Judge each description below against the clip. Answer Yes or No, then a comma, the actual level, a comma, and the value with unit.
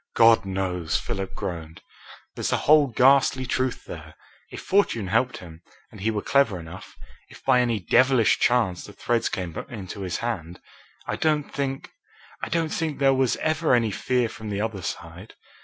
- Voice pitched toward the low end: Yes, low, 115 Hz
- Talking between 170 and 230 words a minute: Yes, average, 175 wpm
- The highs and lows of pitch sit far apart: Yes, wide, 5.9 semitones